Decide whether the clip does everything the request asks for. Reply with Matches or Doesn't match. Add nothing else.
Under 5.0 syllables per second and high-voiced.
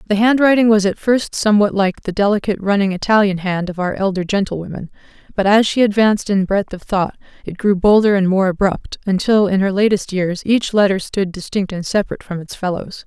Doesn't match